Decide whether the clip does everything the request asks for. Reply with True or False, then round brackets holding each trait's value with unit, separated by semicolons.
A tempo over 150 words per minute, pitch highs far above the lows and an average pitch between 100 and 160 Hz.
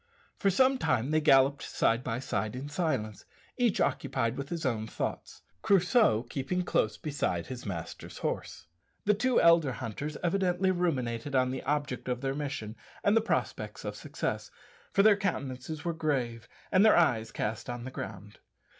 True (165 wpm; 6.8 semitones; 140 Hz)